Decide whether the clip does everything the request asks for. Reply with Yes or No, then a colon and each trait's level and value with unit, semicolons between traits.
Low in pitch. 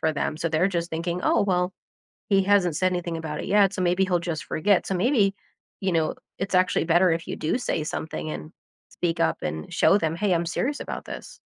No: medium, 175 Hz